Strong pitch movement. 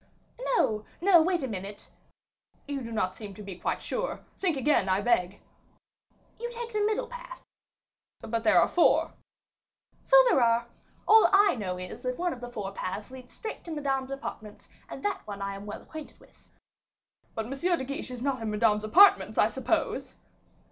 Yes: wide, 8.8 semitones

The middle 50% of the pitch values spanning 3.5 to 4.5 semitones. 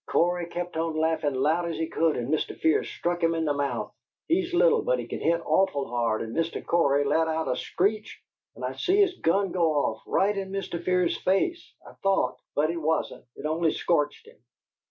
Yes: average, 3.8 semitones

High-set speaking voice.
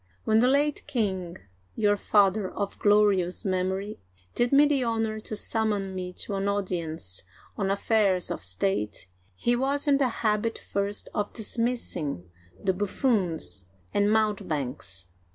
Yes: high, 205 Hz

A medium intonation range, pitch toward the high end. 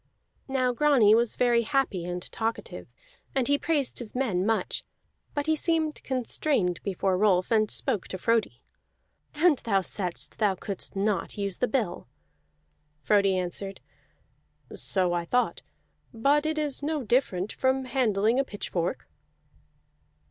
No: wide, 5.7 semitones; high, 225 Hz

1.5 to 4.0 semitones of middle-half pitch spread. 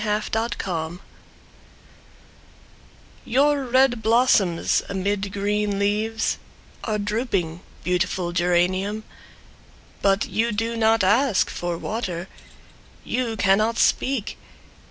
Yes: average, 3.4 semitones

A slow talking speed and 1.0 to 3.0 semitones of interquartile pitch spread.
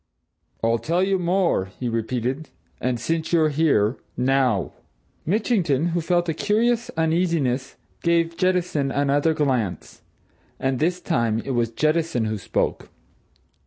No: slow, 125 wpm; wide, 5.5 semitones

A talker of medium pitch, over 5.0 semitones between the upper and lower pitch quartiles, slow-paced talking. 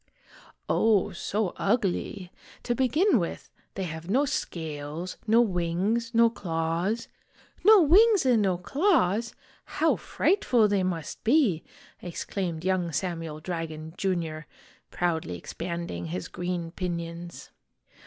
Yes: medium, 180 Hz; wide, 5.4 semitones; slow, 120 wpm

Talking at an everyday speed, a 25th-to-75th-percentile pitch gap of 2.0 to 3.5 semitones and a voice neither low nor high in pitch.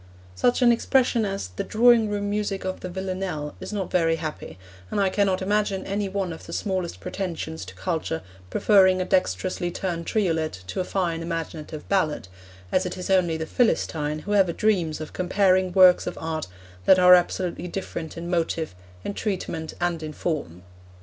Yes: average, 175 wpm; average, 3.2 semitones; medium, 180 Hz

